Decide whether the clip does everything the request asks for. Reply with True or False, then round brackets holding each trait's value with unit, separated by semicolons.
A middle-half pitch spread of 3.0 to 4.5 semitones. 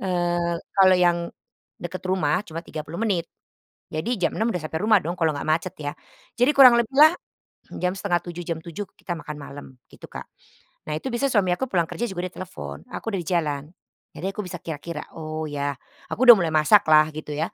True (3.7 semitones)